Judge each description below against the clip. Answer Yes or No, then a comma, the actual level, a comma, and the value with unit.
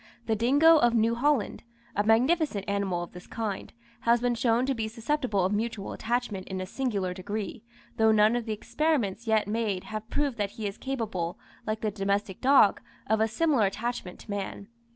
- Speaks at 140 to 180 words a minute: No, average, 190 wpm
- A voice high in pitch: Yes, high, 220 Hz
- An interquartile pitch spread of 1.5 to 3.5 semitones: Yes, average, 3.1 semitones